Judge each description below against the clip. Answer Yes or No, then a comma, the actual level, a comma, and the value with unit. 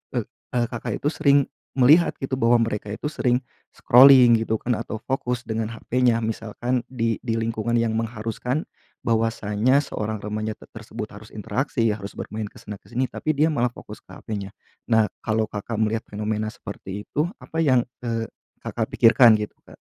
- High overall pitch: No, low, 115 Hz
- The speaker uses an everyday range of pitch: No, narrow, 2.3 semitones